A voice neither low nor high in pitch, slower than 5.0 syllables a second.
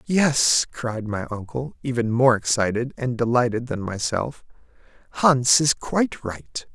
No: low, 120 Hz; 4.1 syllables/s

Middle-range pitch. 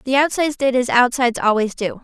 No: very high, 255 Hz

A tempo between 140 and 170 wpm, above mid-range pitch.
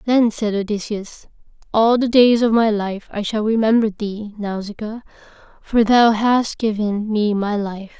Yes: average, 160 wpm; high, 215 Hz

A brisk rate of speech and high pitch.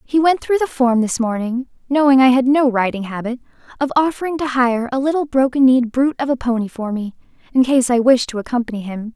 Yes: fast, 225 wpm; very high, 255 Hz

